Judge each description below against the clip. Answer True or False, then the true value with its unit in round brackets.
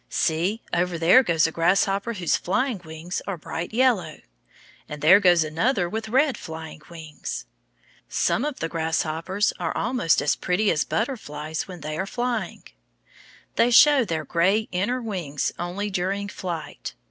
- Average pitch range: True (5.0 semitones)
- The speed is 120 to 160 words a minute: True (150 wpm)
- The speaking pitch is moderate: True (180 Hz)